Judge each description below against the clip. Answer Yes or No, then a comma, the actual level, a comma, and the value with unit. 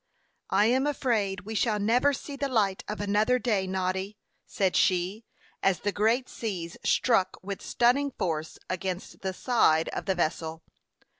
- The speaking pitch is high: Yes, high, 205 Hz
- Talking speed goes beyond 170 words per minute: No, average, 155 wpm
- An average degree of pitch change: Yes, average, 4.1 semitones